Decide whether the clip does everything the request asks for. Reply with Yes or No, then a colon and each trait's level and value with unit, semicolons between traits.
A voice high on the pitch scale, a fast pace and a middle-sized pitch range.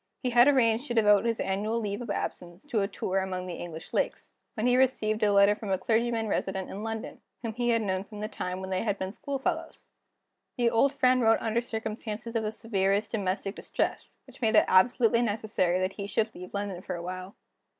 Yes: high, 215 Hz; fast, 220 wpm; average, 3.2 semitones